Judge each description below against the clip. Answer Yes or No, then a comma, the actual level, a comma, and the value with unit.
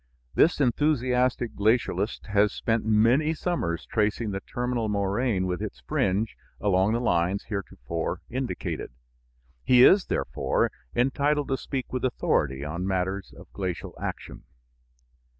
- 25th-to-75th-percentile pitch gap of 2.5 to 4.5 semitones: No, average, 5.0 semitones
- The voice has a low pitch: Yes, low, 110 Hz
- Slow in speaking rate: Yes, slow, 125 wpm